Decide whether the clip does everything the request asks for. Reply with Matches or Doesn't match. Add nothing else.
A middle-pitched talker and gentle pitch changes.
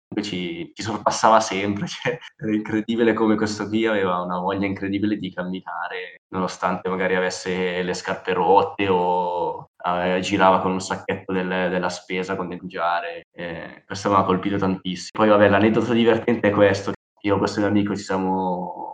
Doesn't match